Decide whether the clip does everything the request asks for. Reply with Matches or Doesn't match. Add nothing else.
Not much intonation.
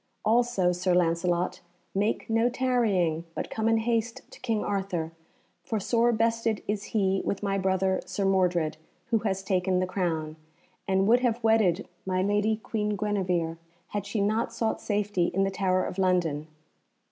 Doesn't match